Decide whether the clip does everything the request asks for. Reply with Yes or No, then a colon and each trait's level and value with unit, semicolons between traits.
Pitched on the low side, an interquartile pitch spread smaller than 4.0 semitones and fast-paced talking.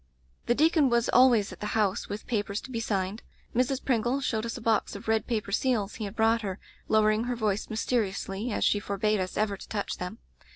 No: high, 220 Hz; average, 2.7 semitones; fast, 220 wpm